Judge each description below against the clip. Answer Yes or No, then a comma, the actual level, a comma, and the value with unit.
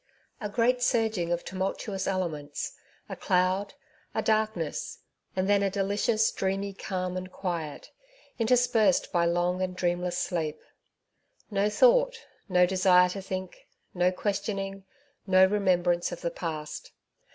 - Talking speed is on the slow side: Yes, slow, 130 wpm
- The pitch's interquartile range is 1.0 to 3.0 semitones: Yes, narrow, 2.4 semitones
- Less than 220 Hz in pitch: Yes, medium, 185 Hz